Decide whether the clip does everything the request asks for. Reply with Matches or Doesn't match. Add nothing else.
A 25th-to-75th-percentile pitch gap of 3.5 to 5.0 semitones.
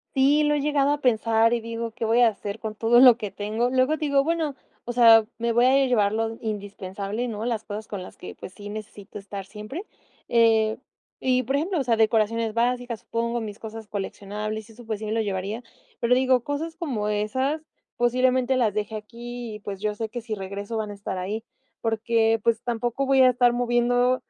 Doesn't match